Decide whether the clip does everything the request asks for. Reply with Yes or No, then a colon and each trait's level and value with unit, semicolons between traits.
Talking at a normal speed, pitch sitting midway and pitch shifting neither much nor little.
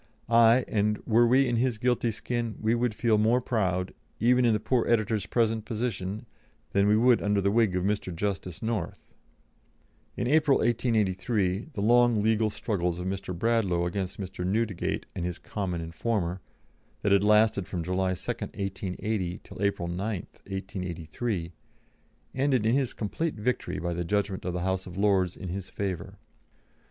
No: average, 165 wpm; low, 105 Hz; average, 3.9 semitones